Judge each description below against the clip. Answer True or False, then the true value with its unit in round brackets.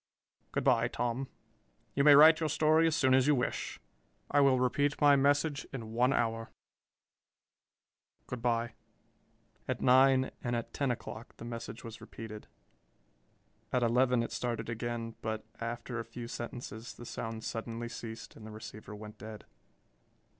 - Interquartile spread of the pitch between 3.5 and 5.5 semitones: False (2.7 semitones)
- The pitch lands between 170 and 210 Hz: False (120 Hz)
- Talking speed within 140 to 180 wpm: True (155 wpm)